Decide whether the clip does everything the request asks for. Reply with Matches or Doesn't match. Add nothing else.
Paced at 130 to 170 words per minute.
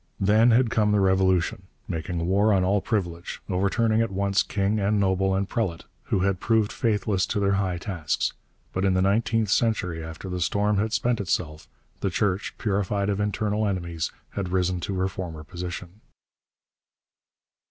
Matches